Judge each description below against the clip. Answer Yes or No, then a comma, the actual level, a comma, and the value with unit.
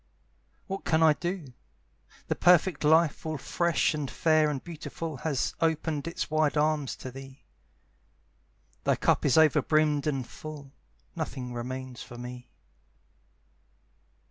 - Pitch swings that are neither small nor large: Yes, average, 3.0 semitones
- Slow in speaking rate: Yes, slow, 130 wpm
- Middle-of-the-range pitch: Yes, medium, 150 Hz